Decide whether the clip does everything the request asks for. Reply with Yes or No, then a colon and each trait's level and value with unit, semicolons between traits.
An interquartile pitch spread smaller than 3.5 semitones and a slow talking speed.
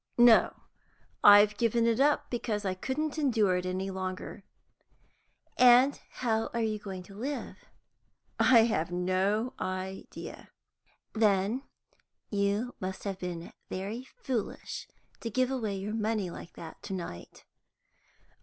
No: average, 4.1 semitones; slow, 125 wpm